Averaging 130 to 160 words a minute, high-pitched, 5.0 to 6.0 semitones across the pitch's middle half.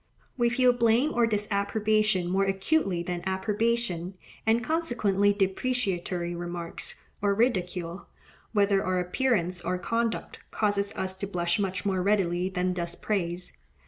No: slow, 135 wpm; high, 195 Hz; average, 3.6 semitones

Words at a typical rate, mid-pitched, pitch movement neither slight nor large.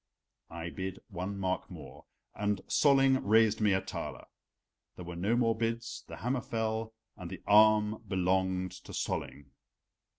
No: average, 145 wpm; low, 105 Hz; average, 3.3 semitones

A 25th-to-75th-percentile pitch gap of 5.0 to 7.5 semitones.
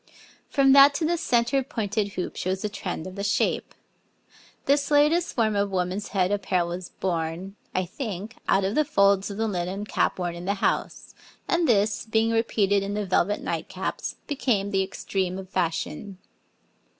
No: average, 3.4 semitones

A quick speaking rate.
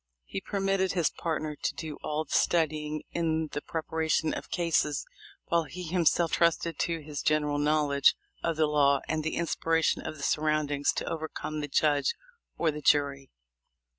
No: average, 170 wpm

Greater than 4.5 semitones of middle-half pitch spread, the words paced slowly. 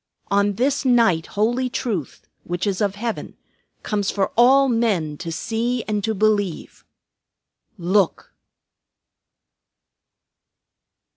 No: average, 3.7 semitones; slow, 100 wpm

